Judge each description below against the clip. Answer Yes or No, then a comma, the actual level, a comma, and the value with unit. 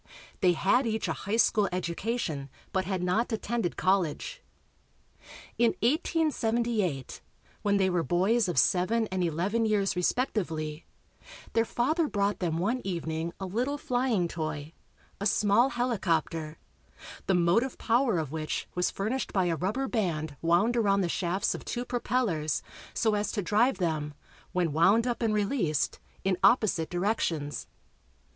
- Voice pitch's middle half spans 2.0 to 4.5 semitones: No, average, 5.3 semitones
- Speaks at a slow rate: No, average, 145 wpm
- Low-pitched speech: No, high, 195 Hz